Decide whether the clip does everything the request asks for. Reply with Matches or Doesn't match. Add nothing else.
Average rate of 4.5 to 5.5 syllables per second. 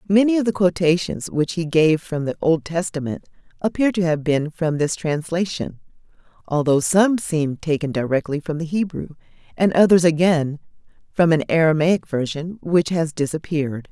Matches